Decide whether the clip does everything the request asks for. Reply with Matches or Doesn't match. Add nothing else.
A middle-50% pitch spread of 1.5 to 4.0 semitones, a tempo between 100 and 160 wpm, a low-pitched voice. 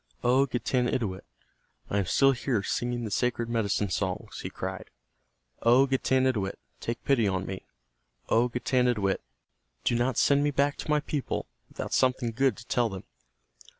Matches